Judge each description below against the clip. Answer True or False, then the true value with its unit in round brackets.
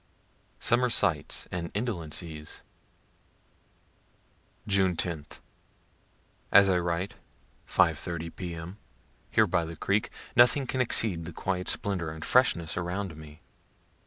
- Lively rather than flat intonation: False (3.5 semitones)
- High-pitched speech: False (90 Hz)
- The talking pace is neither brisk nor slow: False (110 wpm)